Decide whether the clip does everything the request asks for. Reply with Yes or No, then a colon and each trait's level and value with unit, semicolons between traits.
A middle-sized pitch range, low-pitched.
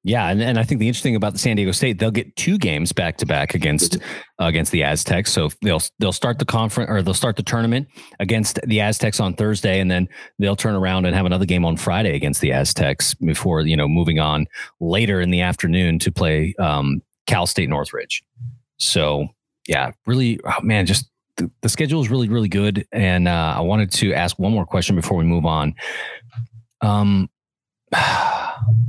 Yes: average, 4.2 semitones; low, 100 Hz